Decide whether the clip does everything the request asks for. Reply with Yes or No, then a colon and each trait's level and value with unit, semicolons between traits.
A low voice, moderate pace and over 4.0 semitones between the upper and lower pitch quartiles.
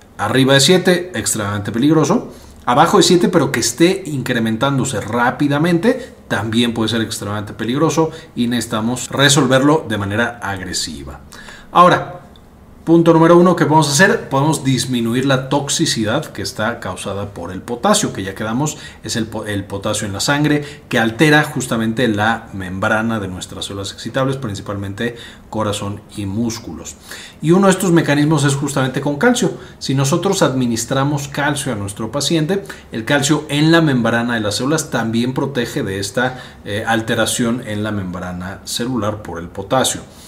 Yes: low, 120 Hz; average, 150 wpm; wide, 5.6 semitones